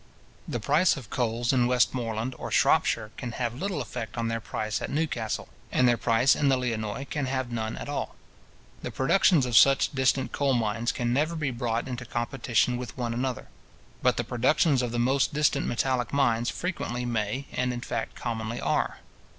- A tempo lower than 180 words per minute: No, average, 185 wpm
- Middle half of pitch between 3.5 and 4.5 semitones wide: No, narrow, 2.5 semitones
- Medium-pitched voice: No, low, 125 Hz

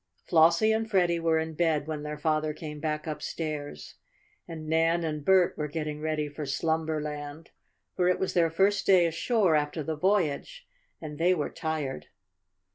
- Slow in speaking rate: No, average, 165 wpm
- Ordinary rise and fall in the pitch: No, narrow, 2.2 semitones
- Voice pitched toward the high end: No, medium, 160 Hz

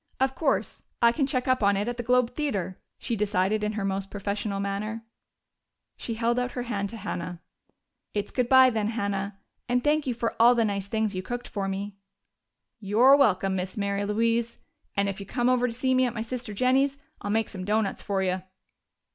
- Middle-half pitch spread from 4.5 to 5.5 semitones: No, average, 3.7 semitones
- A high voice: Yes, high, 220 Hz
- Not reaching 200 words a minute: No, fast, 205 wpm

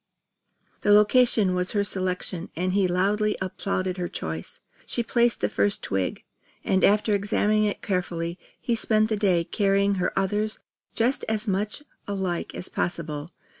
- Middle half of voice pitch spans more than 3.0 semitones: No, narrow, 2.6 semitones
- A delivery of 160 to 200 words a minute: No, average, 150 wpm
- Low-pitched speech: No, high, 195 Hz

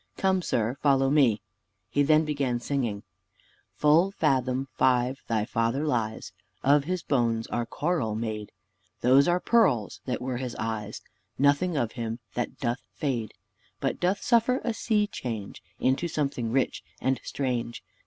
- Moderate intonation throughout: Yes, average, 4.5 semitones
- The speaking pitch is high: No, low, 130 Hz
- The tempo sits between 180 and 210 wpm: No, average, 145 wpm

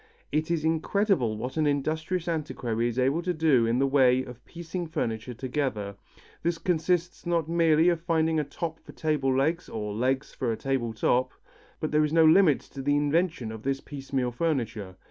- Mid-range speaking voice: Yes, medium, 145 Hz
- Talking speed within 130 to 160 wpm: No, average, 185 wpm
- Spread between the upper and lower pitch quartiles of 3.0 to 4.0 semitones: No, average, 4.5 semitones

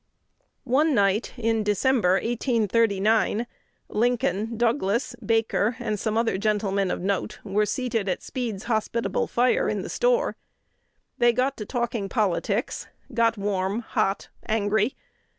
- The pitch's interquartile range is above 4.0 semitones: No, average, 2.8 semitones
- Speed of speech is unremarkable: No, slow, 125 wpm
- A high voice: Yes, high, 225 Hz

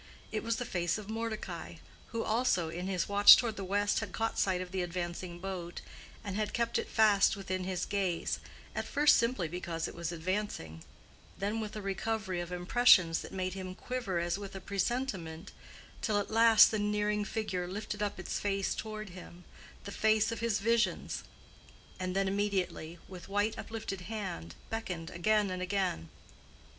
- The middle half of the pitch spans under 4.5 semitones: Yes, average, 3.3 semitones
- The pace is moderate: Yes, average, 170 wpm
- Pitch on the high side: Yes, high, 195 Hz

